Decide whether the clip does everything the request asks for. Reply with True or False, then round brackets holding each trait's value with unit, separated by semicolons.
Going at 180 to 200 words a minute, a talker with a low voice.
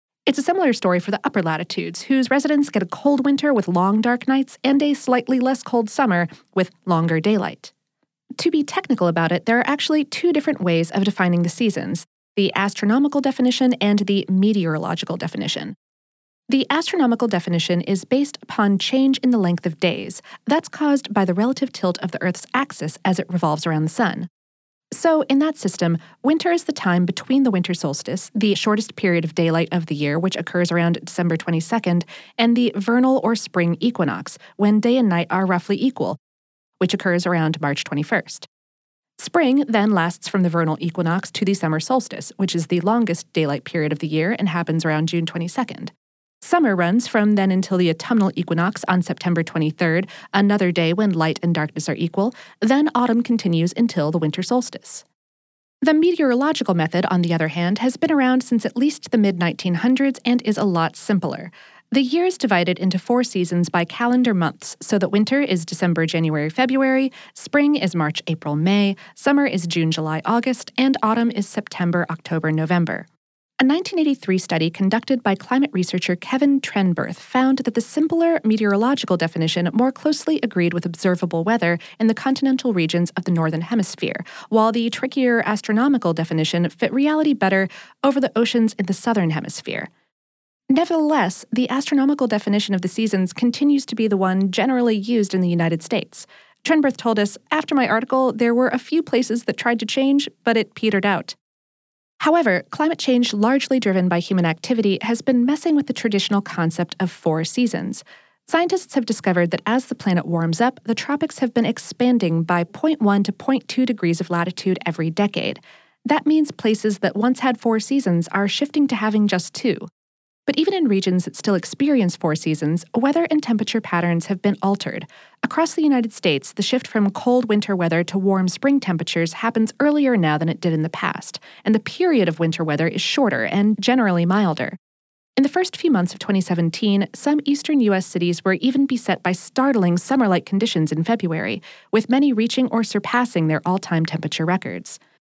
False (185 wpm; 205 Hz)